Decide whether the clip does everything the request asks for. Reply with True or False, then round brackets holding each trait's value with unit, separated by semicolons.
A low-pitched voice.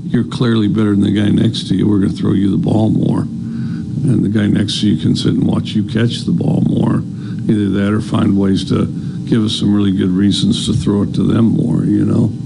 True (105 Hz)